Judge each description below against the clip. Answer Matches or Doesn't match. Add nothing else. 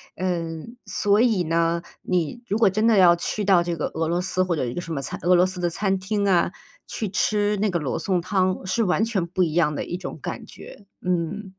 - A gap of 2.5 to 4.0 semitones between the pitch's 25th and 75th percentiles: Matches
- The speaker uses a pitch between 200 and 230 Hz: Doesn't match